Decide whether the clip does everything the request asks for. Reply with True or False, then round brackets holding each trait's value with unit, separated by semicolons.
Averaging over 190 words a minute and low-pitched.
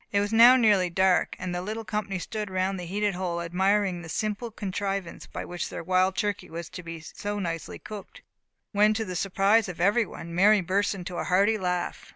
False (200 wpm; 195 Hz)